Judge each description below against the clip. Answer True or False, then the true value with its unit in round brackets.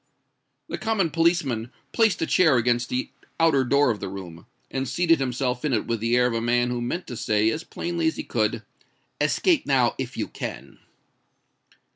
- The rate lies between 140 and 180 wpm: False (190 wpm)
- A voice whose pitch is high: False (125 Hz)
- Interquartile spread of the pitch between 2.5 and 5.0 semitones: False (5.6 semitones)